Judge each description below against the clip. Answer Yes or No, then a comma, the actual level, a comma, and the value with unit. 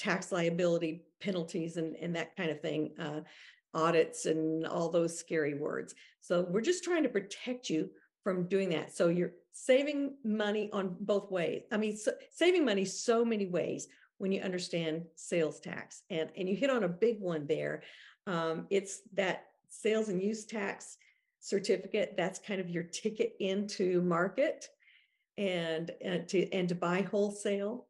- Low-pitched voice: No, medium, 185 Hz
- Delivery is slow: No, average, 165 wpm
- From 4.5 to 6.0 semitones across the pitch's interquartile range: No, average, 4.0 semitones